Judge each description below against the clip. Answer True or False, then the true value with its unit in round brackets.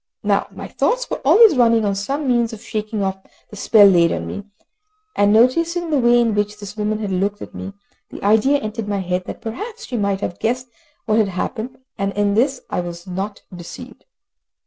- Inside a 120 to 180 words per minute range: False (205 wpm)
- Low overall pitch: False (215 Hz)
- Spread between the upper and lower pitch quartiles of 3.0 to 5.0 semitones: True (3.4 semitones)